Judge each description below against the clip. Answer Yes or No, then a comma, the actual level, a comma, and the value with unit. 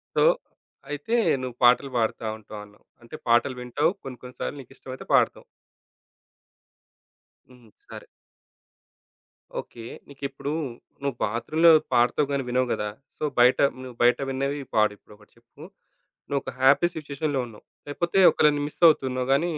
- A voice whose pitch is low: Yes, low, 130 Hz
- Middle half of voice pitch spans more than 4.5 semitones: No, average, 3.3 semitones